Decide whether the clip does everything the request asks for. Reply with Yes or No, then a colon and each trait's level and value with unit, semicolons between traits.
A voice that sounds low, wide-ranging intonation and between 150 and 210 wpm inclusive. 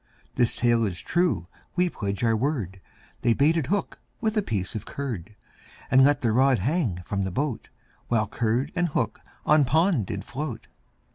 Yes: low, 125 Hz; wide, 6.1 semitones; average, 170 wpm